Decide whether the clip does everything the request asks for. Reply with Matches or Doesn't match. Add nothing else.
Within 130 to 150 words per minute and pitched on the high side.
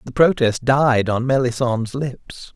Doesn't match